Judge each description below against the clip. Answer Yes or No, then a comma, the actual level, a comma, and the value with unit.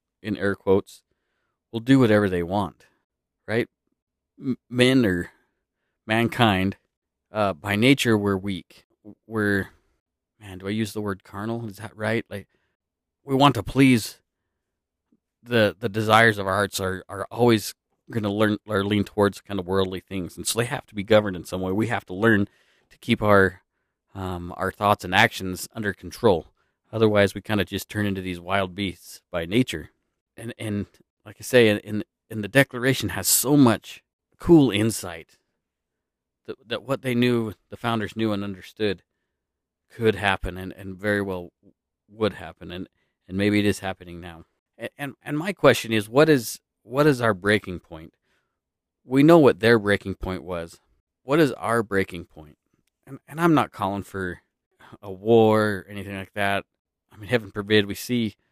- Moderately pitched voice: No, low, 100 Hz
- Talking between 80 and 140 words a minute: No, average, 175 wpm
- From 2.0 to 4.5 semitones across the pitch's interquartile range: Yes, average, 3.2 semitones